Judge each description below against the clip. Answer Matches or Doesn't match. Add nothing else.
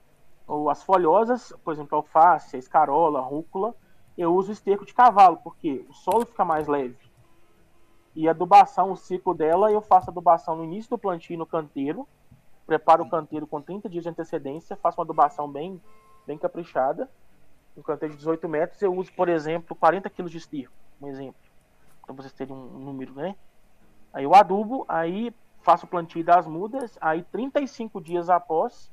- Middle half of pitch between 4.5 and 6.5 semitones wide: Doesn't match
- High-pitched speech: Doesn't match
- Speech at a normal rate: Matches